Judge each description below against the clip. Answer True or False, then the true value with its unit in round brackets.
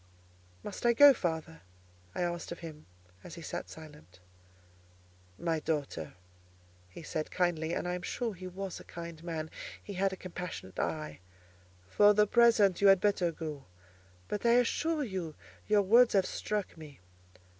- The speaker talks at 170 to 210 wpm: False (155 wpm)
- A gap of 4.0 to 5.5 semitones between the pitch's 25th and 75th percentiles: True (4.5 semitones)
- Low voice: False (175 Hz)